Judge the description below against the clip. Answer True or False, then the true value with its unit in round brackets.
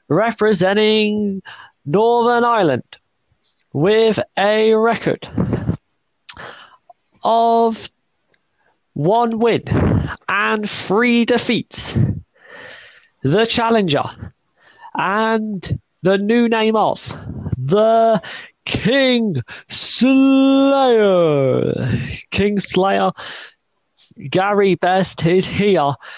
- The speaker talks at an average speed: False (65 wpm)